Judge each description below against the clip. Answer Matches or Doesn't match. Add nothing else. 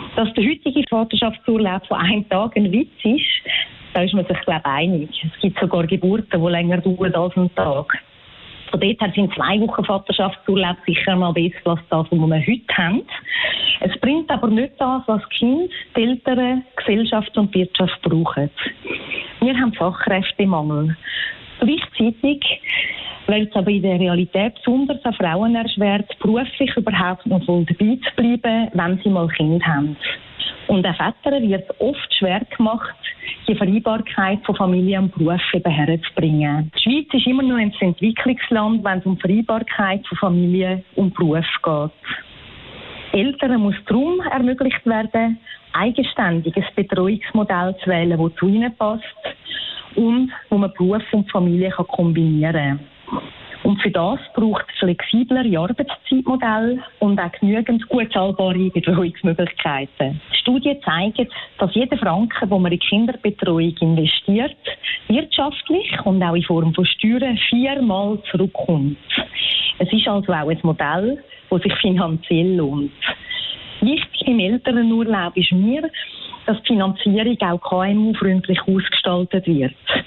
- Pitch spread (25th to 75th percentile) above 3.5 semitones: Matches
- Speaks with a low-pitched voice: Doesn't match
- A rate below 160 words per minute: Matches